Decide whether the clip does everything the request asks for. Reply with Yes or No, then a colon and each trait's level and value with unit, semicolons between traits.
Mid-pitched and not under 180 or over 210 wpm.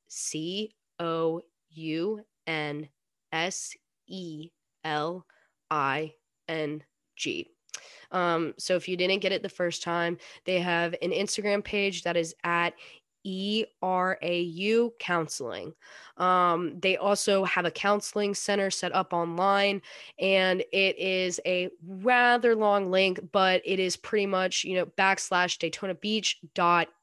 No: medium, 180 Hz; slow, 135 wpm